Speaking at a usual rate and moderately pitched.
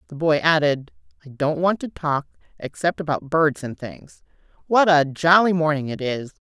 Yes: average, 175 wpm; medium, 155 Hz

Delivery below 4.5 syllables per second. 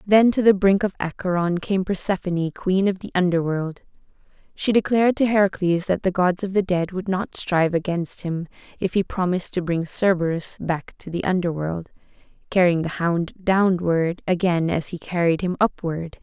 No: 5.1 syllables/s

